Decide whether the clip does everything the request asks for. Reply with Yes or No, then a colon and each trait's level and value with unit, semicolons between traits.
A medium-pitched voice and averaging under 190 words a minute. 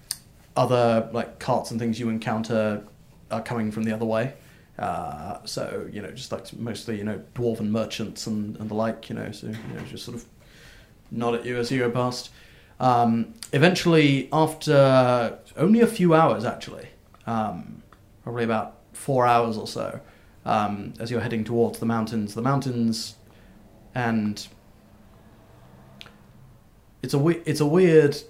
No: low, 115 Hz; average, 155 wpm